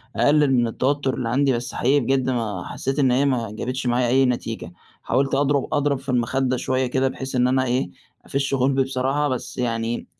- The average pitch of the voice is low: Yes, low, 130 Hz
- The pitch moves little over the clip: Yes, narrow, 1.9 semitones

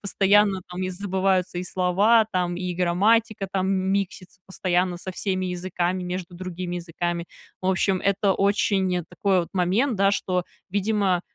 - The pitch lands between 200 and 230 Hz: No, medium, 185 Hz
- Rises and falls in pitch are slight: Yes, narrow, 1.7 semitones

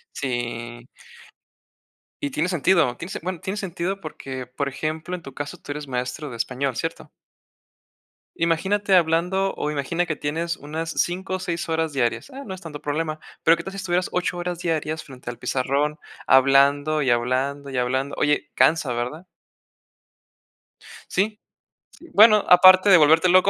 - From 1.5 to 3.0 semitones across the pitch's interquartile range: No, average, 4.6 semitones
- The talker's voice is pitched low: No, medium, 155 Hz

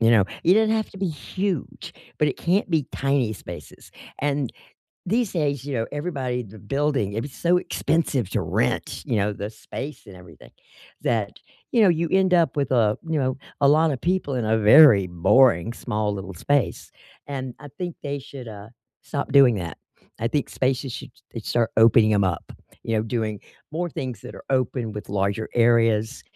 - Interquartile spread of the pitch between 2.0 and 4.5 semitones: No, wide, 5.5 semitones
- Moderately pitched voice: No, low, 130 Hz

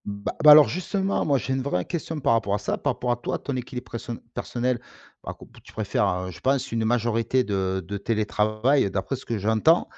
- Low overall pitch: Yes, low, 115 Hz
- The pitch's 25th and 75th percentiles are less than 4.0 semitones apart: No, average, 4.3 semitones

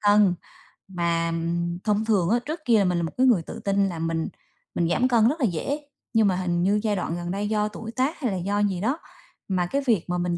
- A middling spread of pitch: Yes, average, 4.2 semitones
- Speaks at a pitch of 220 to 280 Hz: No, high, 200 Hz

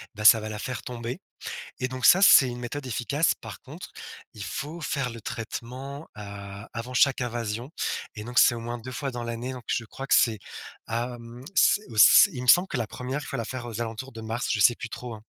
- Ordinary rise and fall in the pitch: No, narrow, 2.2 semitones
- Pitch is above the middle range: No, low, 120 Hz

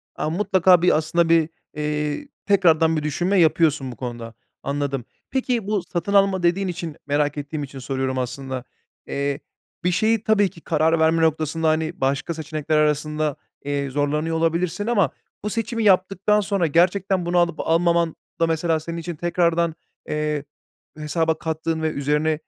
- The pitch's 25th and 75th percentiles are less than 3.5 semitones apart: Yes, average, 2.8 semitones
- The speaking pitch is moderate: Yes, medium, 160 Hz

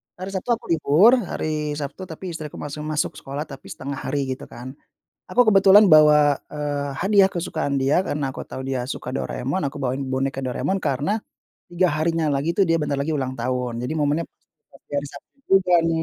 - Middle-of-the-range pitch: Yes, medium, 150 Hz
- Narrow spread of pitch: No, average, 3.5 semitones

